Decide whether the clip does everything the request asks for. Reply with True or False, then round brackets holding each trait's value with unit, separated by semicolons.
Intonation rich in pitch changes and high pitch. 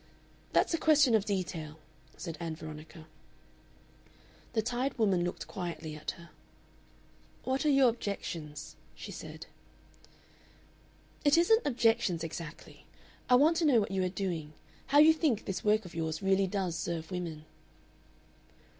True (7.2 semitones; 195 Hz)